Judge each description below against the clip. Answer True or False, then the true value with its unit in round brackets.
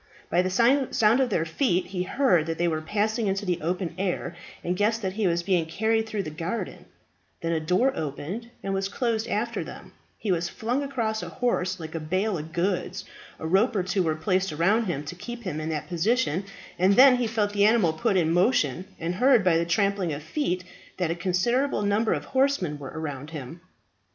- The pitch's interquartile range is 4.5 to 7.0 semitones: True (4.9 semitones)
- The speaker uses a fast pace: True (210 wpm)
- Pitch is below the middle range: False (185 Hz)